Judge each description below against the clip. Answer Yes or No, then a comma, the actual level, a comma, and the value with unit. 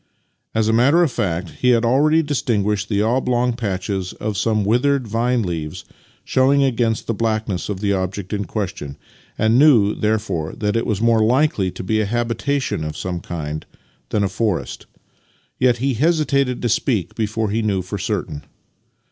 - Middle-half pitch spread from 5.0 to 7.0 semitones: No, average, 4.0 semitones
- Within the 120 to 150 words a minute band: No, average, 170 wpm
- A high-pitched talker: No, low, 110 Hz